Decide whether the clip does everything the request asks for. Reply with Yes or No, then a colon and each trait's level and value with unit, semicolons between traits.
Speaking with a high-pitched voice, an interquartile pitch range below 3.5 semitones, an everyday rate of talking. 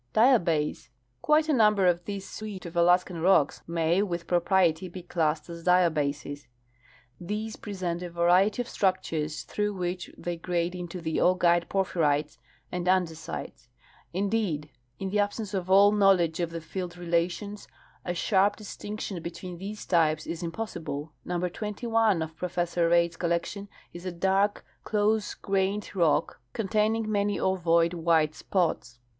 No: medium, 180 Hz; average, 3.1 semitones; average, 150 wpm